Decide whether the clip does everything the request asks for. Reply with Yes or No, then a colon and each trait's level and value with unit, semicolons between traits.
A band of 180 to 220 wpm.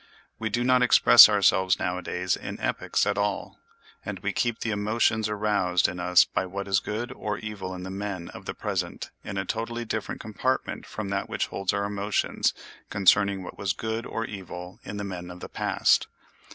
Yes: average, 190 wpm